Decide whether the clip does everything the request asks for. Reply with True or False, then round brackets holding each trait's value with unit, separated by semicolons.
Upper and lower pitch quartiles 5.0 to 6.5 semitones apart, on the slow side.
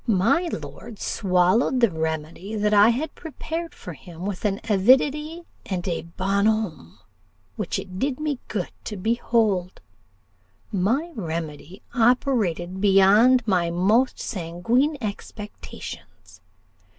True (5.3 semitones; 115 wpm)